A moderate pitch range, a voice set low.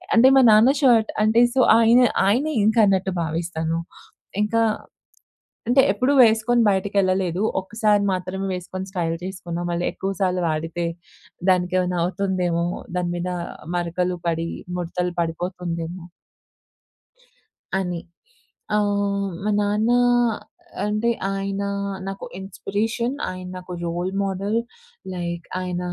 No: average, 3.0 semitones; medium, 185 Hz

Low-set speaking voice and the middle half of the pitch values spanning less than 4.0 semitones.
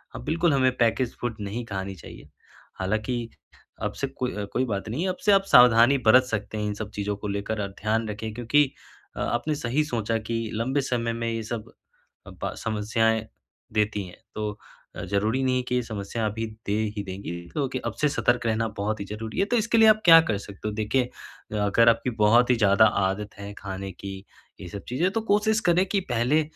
Yes: low, 115 Hz; average, 3.6 semitones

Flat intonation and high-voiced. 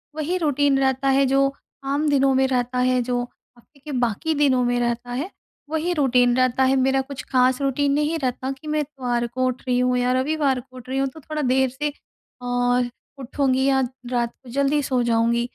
Yes: narrow, 2.2 semitones; very high, 260 Hz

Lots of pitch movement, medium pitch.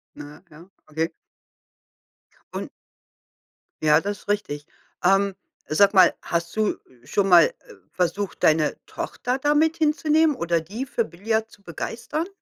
No: wide, 6.0 semitones; high, 200 Hz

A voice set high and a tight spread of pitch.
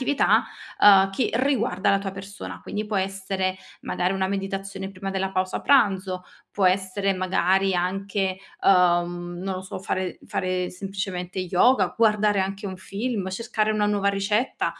Yes: high, 195 Hz; narrow, 1.4 semitones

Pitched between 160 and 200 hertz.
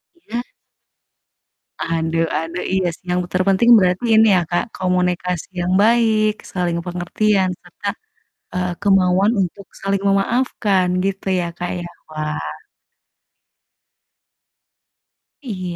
Yes: medium, 185 Hz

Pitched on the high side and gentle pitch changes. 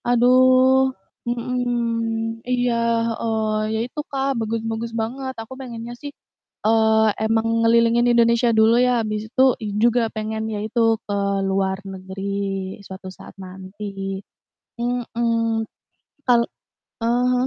Yes: high, 230 Hz; narrow, 2.0 semitones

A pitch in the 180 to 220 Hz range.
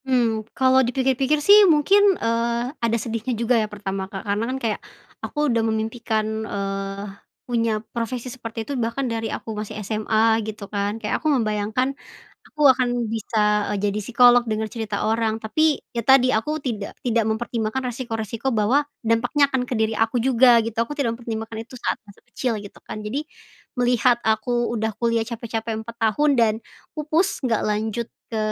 No: high, 230 Hz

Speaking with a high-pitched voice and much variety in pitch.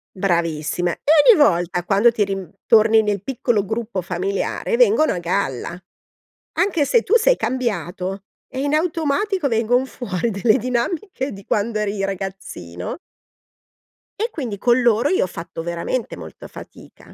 Yes: high, 220 Hz; wide, 6.2 semitones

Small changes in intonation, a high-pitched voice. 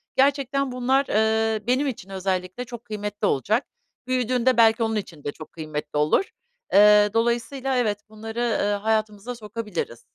No: average, 3.3 semitones; high, 220 Hz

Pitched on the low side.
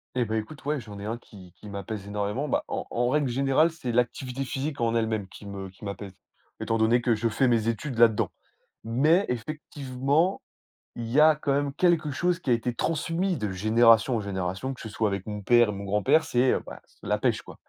Yes: low, 120 Hz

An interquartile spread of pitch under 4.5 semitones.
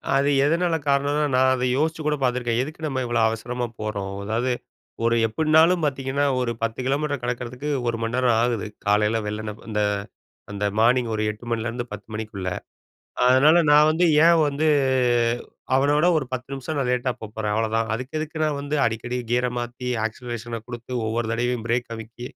Yes: average, 3.9 semitones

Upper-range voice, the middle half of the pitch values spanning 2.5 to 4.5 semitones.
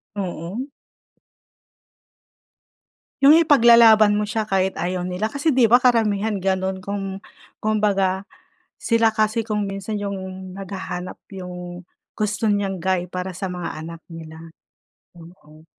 Yes: high, 195 Hz; average, 3.0 semitones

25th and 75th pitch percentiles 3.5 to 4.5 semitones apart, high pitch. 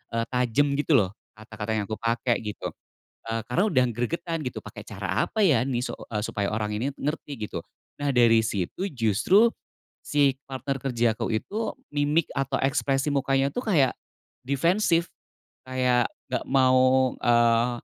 No: average, 3.8 semitones; low, 130 Hz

